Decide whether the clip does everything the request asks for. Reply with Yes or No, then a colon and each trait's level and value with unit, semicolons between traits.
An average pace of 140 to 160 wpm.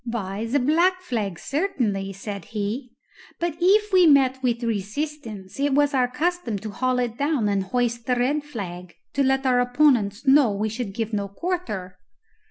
No: average, 175 wpm